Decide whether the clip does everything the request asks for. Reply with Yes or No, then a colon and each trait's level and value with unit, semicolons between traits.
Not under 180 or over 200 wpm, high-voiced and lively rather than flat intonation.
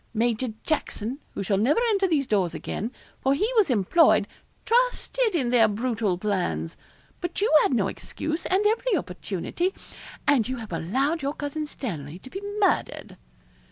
No: average, 155 wpm; very high, 260 Hz; wide, 8.6 semitones